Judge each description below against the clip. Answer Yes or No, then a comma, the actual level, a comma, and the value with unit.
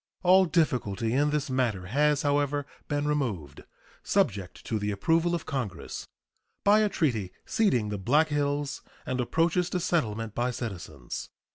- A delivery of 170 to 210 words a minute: No, average, 145 wpm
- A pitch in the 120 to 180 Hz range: Yes, medium, 140 Hz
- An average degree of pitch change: No, wide, 6.6 semitones